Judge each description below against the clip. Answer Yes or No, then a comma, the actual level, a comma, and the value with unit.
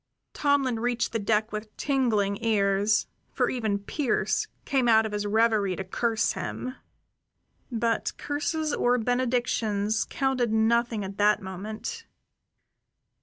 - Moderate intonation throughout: Yes, average, 3.0 semitones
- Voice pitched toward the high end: Yes, high, 225 Hz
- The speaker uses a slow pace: Yes, slow, 120 wpm